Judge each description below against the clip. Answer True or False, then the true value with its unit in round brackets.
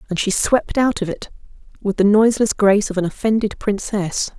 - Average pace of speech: True (190 wpm)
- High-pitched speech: True (205 Hz)